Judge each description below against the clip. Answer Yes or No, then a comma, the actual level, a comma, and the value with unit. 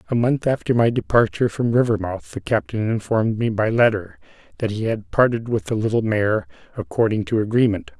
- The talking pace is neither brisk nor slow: Yes, average, 180 wpm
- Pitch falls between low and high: No, low, 110 Hz